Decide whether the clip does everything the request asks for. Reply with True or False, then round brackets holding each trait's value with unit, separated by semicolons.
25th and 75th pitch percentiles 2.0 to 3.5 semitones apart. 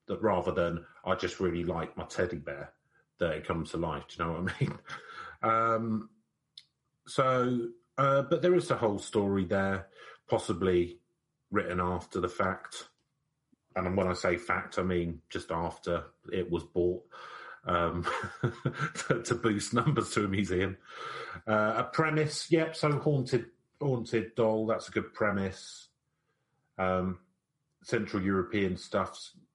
False (5.2 semitones)